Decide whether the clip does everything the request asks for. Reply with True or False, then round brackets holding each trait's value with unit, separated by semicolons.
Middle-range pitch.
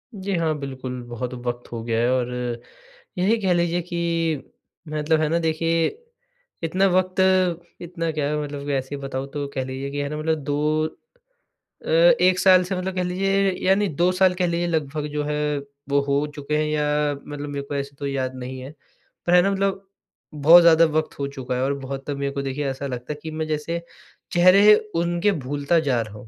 True (155 Hz)